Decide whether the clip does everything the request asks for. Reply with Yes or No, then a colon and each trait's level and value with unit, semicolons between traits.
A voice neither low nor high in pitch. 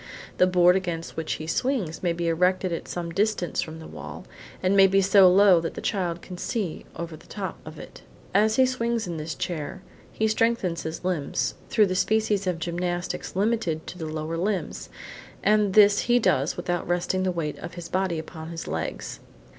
Yes: medium, 180 Hz